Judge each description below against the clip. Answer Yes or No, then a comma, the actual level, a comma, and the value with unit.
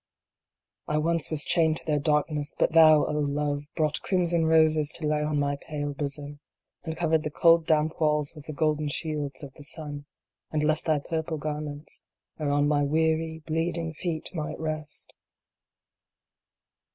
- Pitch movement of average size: No, narrow, 1.5 semitones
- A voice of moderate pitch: Yes, medium, 155 Hz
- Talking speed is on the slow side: No, average, 160 wpm